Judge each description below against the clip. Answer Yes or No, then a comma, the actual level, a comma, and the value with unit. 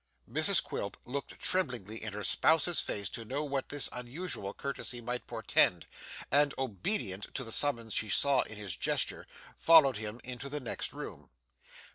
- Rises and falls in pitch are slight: No, average, 4.8 semitones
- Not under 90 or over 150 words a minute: No, average, 160 wpm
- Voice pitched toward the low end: Yes, low, 125 Hz